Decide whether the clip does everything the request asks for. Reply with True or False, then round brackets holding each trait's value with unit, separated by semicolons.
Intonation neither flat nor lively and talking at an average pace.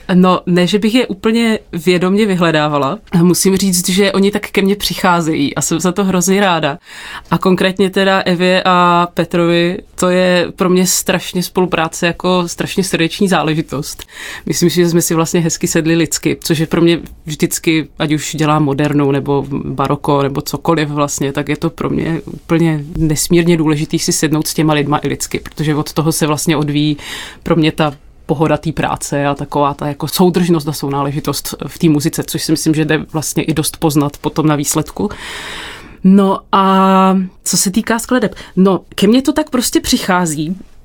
False (3.3 semitones; 180 wpm)